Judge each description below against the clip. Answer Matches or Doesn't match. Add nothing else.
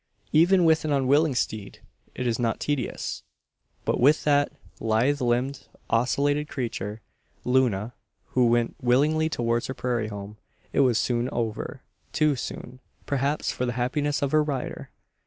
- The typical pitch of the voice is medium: Doesn't match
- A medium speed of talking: Matches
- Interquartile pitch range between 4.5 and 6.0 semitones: Doesn't match